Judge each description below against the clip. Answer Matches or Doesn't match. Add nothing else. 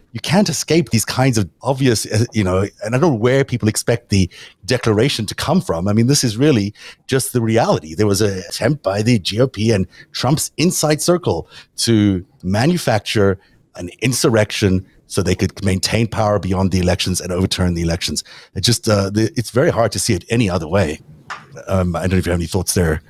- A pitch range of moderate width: Matches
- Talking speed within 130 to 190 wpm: Doesn't match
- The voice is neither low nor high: Doesn't match